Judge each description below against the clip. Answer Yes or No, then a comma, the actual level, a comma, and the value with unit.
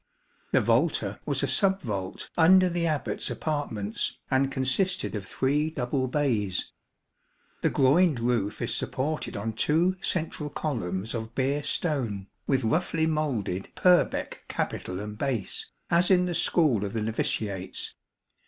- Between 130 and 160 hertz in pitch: Yes, low, 135 Hz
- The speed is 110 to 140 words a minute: Yes, slow, 135 wpm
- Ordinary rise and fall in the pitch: No, wide, 6.7 semitones